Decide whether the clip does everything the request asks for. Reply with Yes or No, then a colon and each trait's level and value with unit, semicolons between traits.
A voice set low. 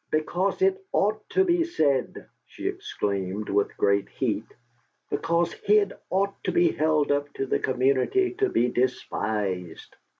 No: medium, 155 Hz